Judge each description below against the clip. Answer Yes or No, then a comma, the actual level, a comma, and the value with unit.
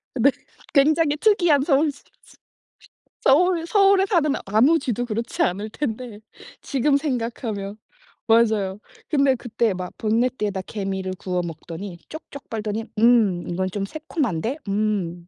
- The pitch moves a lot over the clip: Yes, wide, 6.3 semitones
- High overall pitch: Yes, high, 230 Hz